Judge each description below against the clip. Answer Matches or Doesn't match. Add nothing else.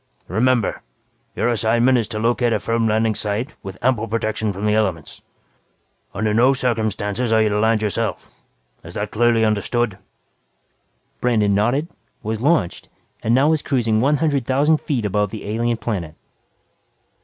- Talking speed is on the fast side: Doesn't match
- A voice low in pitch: Matches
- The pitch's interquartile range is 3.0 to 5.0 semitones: Doesn't match